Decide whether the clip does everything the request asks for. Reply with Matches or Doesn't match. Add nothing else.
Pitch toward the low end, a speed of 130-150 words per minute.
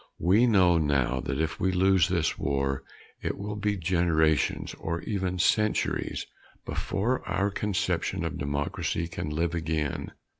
Matches